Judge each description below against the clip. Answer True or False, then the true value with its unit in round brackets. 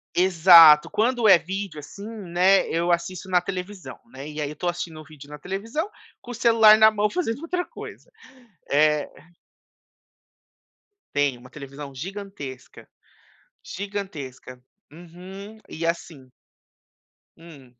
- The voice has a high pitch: False (175 Hz)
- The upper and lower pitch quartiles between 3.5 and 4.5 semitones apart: False (5.3 semitones)